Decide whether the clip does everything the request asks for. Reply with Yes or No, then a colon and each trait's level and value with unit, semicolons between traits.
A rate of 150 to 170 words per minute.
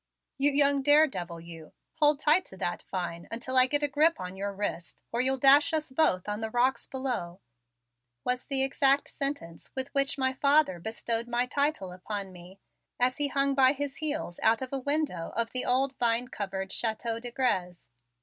No: average, 190 wpm